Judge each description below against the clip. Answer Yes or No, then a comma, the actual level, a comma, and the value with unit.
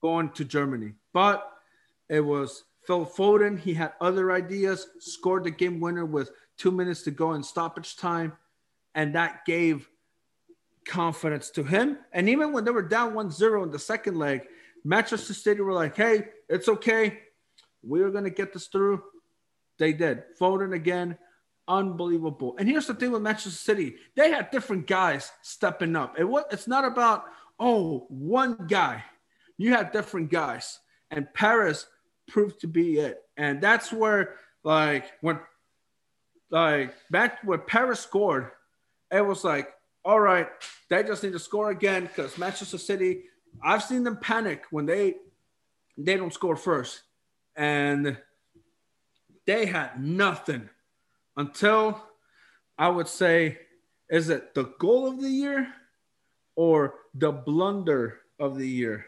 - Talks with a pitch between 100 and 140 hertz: No, medium, 185 Hz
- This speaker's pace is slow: No, average, 145 wpm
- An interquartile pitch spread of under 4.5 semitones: No, average, 5.1 semitones